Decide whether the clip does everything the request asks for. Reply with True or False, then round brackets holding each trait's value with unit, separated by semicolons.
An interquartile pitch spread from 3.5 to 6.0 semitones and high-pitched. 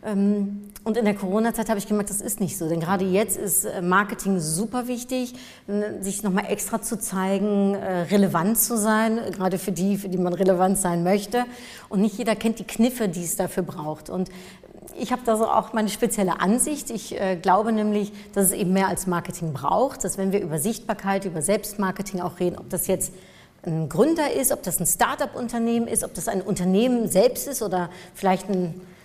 False (3.0 semitones; 200 Hz)